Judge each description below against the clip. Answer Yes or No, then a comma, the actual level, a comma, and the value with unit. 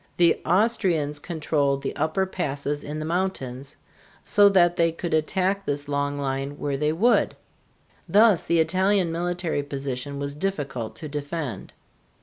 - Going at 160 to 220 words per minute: No, average, 140 wpm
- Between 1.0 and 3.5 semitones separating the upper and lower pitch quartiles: No, average, 4.0 semitones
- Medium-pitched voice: Yes, medium, 155 Hz